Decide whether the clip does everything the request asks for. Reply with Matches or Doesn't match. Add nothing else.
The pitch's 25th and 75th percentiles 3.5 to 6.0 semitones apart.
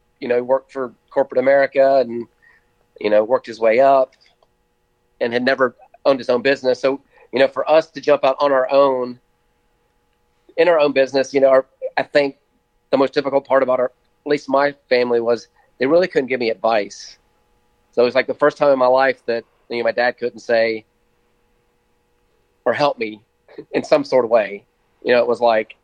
Doesn't match